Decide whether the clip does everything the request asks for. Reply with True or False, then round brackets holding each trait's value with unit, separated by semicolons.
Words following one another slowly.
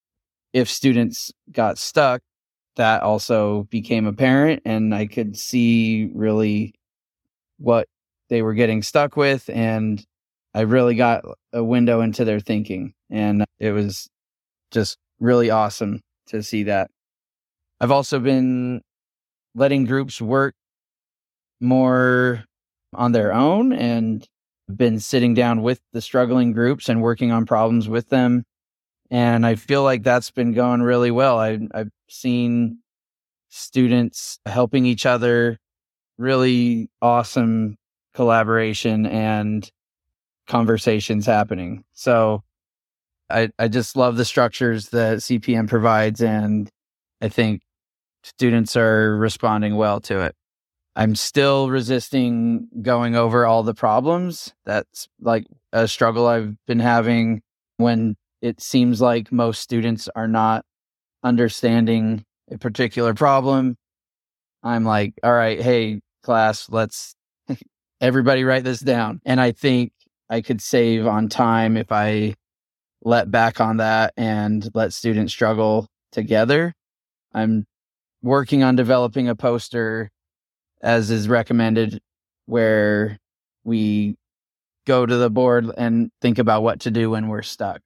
True (125 wpm)